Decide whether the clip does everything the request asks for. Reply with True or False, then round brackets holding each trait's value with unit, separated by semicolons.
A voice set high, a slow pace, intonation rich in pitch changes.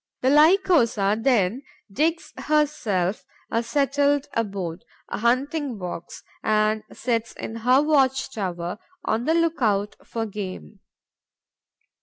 True (230 Hz; 115 wpm; 6.0 semitones)